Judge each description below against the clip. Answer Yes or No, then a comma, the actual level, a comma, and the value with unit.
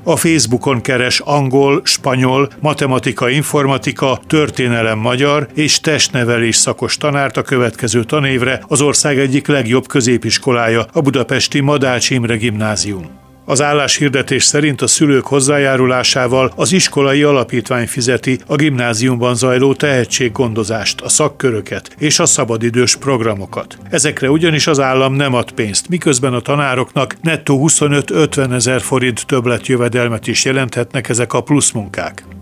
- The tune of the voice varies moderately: Yes, average, 3.0 semitones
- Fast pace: No, average, 125 wpm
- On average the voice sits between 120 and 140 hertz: Yes, low, 130 Hz